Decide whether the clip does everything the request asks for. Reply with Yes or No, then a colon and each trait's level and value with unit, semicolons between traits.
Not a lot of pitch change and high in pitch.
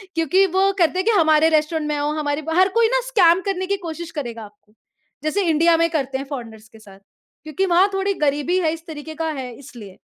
No: average, 4.0 semitones; very high, 315 Hz